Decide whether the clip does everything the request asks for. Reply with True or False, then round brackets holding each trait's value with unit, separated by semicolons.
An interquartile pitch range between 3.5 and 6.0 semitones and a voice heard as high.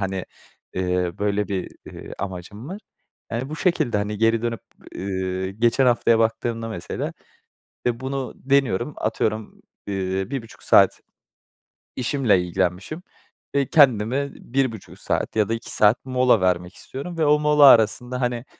False (5.2 semitones; 115 Hz)